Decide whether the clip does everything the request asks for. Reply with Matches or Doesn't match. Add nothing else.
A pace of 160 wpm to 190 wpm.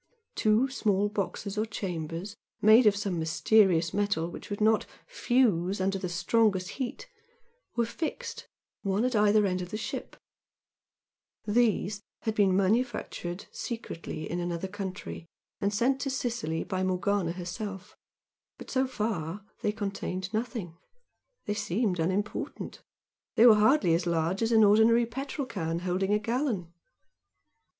Doesn't match